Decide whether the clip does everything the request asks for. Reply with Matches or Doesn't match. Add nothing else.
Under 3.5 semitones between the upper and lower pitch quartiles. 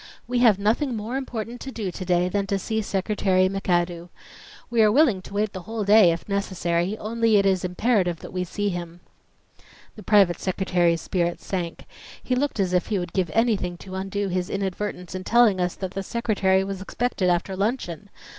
Matches